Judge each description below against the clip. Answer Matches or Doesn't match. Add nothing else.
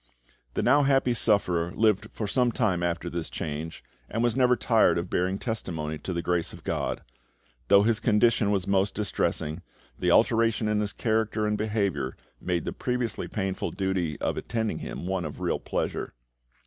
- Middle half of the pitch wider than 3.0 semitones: Matches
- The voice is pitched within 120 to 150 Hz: Doesn't match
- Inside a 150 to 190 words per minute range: Matches